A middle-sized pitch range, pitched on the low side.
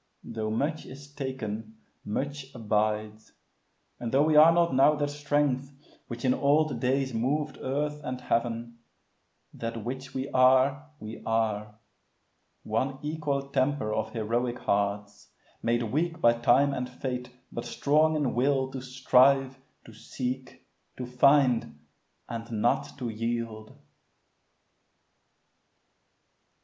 Yes: average, 3.5 semitones; low, 130 Hz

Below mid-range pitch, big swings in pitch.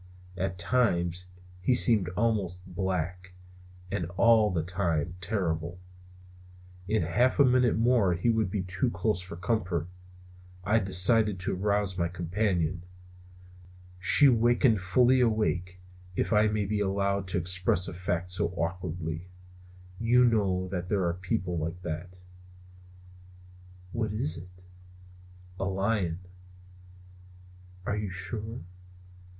No: very low, 95 Hz; average, 3.5 semitones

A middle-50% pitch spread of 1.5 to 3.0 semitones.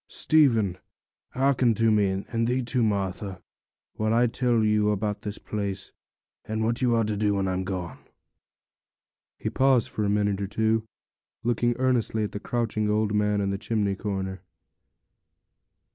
Yes: narrow, 2.5 semitones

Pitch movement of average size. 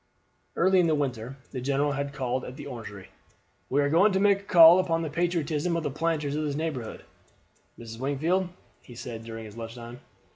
Yes: average, 5.0 semitones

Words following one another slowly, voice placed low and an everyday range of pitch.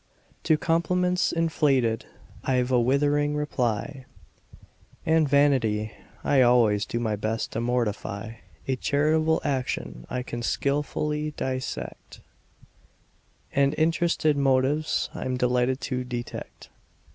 Yes: slow, 105 wpm; low, 130 Hz; average, 3.8 semitones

